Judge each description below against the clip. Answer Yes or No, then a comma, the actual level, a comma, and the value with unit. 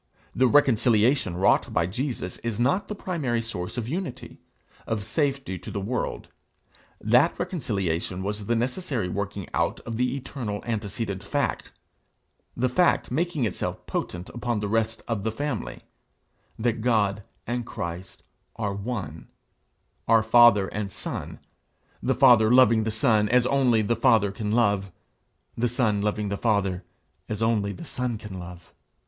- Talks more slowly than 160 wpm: Yes, average, 150 wpm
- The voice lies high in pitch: No, low, 115 Hz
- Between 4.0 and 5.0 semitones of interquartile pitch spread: No, average, 3.6 semitones